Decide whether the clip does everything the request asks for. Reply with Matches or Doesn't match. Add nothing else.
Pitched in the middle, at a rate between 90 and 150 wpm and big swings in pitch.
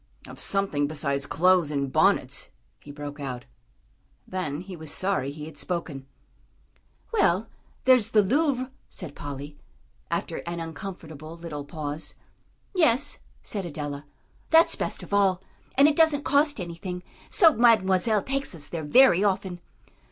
Matches